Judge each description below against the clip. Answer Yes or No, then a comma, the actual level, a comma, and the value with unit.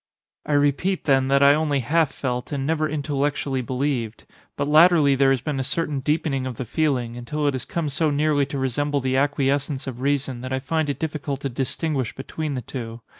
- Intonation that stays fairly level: Yes, narrow, 2.2 semitones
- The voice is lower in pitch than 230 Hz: Yes, medium, 140 Hz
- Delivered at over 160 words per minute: Yes, fast, 205 wpm